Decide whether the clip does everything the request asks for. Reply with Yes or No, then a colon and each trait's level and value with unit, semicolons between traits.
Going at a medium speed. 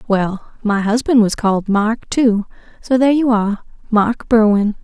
Yes: average, 150 wpm